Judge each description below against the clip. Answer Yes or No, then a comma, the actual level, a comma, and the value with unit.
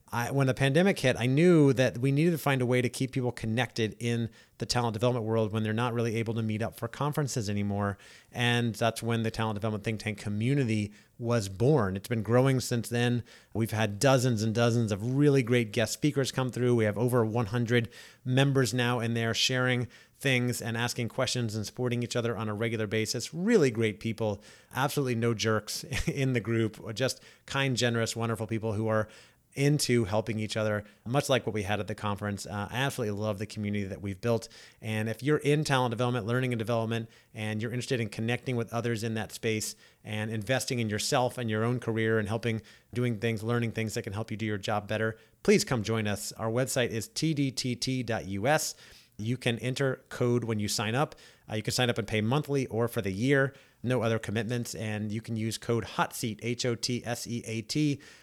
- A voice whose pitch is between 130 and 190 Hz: No, low, 115 Hz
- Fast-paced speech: Yes, fast, 210 wpm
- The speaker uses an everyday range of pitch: No, narrow, 2.3 semitones